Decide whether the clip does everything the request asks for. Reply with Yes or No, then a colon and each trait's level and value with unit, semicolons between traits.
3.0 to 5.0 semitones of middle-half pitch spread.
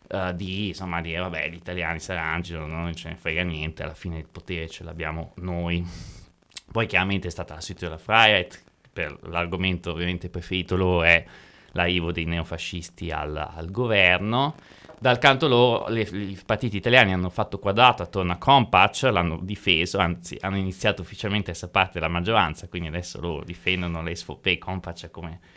No: narrow, 2.4 semitones